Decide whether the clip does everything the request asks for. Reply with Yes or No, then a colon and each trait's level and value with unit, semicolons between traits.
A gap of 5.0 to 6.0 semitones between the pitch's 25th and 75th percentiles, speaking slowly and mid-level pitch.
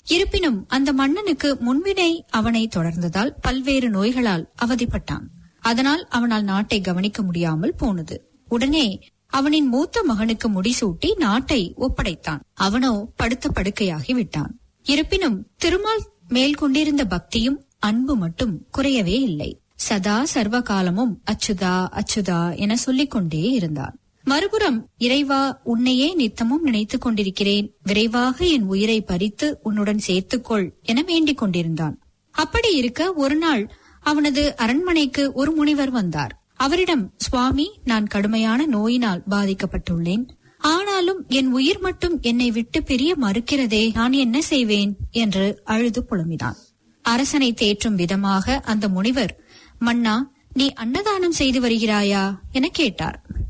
No: wide, 5.4 semitones; slow, 110 wpm; high, 240 Hz